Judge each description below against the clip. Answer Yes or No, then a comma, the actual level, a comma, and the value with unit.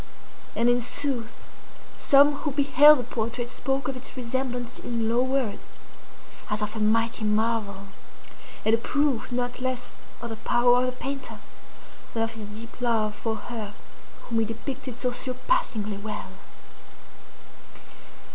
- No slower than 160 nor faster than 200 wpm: No, average, 145 wpm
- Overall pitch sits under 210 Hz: No, high, 240 Hz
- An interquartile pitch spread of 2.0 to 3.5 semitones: Yes, narrow, 2.6 semitones